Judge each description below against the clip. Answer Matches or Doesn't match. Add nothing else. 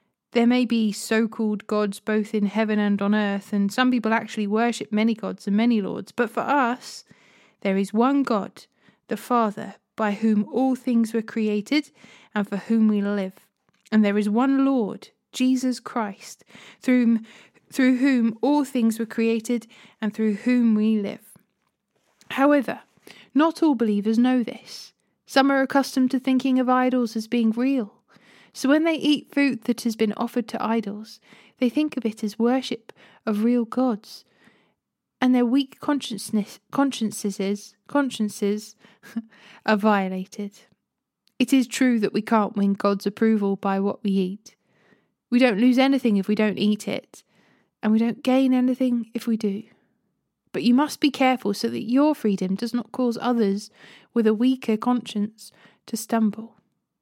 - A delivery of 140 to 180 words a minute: Matches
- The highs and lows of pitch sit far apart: Doesn't match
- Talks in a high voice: Matches